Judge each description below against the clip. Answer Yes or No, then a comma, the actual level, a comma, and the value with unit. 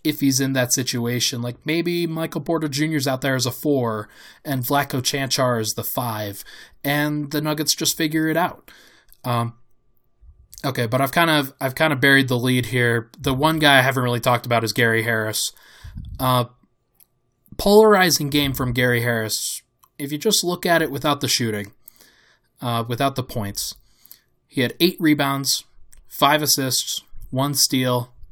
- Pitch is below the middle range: Yes, low, 130 Hz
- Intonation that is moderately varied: Yes, average, 3.7 semitones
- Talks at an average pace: Yes, average, 170 wpm